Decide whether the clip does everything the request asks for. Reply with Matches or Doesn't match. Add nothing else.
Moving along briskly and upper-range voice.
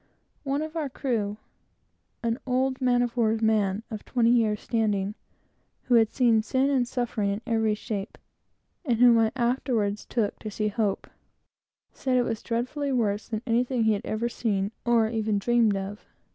Doesn't match